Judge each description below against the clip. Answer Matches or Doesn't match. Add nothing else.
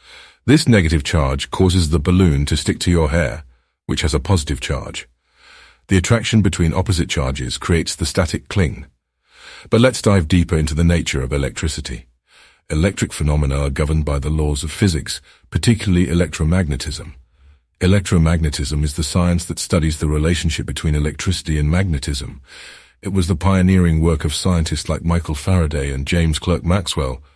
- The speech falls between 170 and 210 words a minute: Doesn't match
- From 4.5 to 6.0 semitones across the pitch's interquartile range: Doesn't match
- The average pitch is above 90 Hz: Doesn't match